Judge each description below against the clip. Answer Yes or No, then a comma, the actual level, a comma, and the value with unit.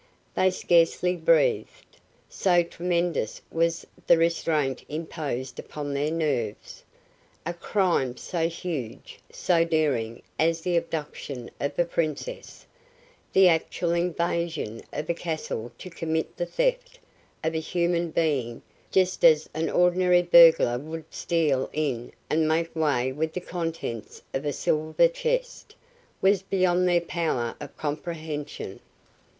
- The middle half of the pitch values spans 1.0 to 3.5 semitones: Yes, average, 2.9 semitones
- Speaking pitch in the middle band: Yes, medium, 165 Hz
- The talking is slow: Yes, slow, 125 wpm